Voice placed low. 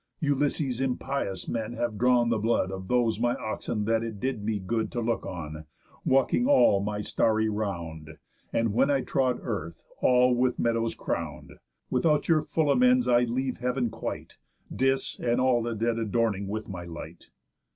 Yes: low, 115 Hz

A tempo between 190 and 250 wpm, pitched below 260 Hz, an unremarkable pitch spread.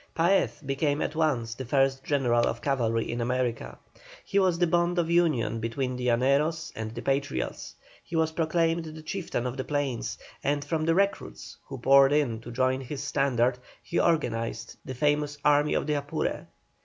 No: average, 180 wpm; medium, 140 Hz; average, 4.2 semitones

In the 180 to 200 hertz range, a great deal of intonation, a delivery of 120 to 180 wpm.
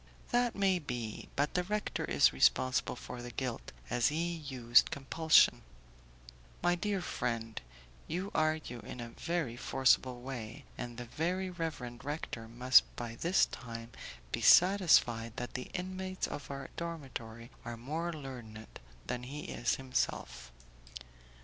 No: low, 130 Hz; wide, 5.9 semitones; slow, 135 wpm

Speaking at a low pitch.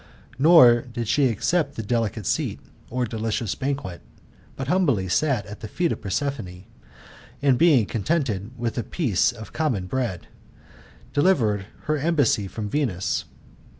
Yes: low, 120 Hz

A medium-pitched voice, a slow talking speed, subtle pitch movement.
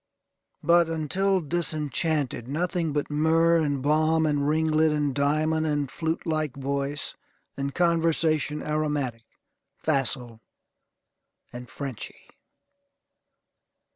Yes: medium, 150 Hz; slow, 95 wpm; narrow, 2.2 semitones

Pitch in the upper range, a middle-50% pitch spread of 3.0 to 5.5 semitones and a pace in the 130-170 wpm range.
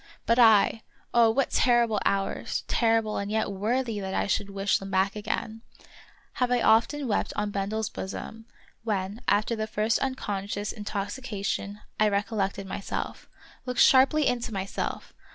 No: high, 215 Hz; narrow, 2.6 semitones; average, 160 wpm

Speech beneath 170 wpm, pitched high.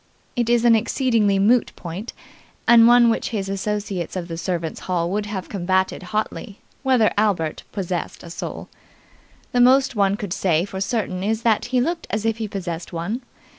No: average, 175 wpm; high, 205 Hz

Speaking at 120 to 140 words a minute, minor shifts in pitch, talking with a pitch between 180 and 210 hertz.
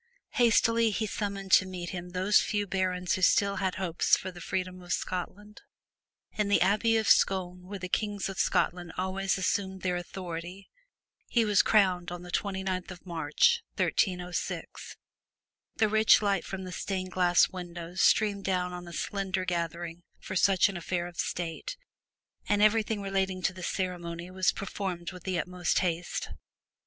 No: average, 165 wpm; narrow, 1.9 semitones; medium, 185 Hz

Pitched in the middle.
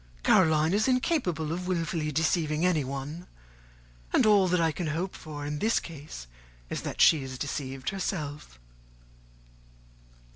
Yes: medium, 160 Hz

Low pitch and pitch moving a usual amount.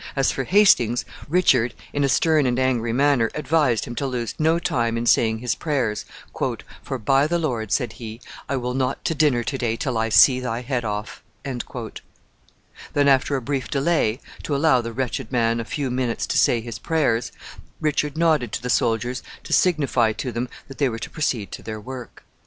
Yes: low, 125 Hz; average, 3.6 semitones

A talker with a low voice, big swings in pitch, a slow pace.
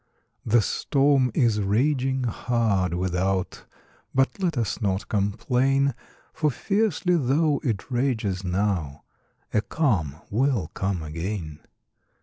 Yes: low, 115 Hz; wide, 6.2 semitones; slow, 110 wpm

